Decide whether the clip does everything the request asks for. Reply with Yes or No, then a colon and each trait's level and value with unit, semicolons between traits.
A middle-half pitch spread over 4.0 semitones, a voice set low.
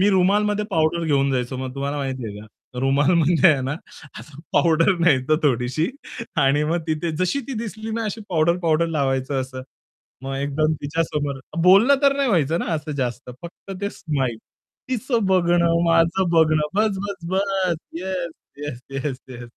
No: average, 5.2 semitones; medium, 160 Hz